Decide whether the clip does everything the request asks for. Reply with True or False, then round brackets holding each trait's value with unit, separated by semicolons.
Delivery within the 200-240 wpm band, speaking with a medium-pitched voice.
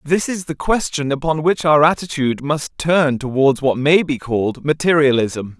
False (170 wpm; 150 Hz)